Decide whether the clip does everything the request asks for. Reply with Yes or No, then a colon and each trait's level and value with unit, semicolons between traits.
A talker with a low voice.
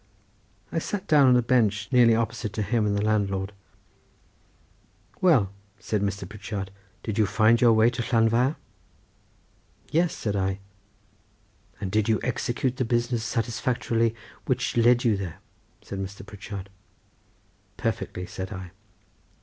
Yes: low, 110 Hz